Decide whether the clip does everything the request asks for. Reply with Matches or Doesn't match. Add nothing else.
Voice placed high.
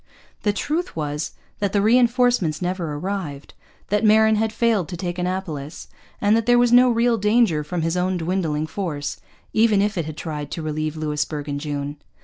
Doesn't match